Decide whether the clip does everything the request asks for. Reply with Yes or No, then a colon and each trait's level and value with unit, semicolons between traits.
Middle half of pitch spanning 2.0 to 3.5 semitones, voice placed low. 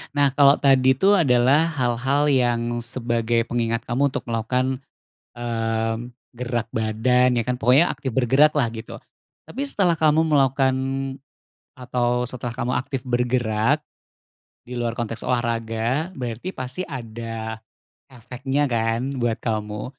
Yes: narrow, 2.5 semitones; low, 125 Hz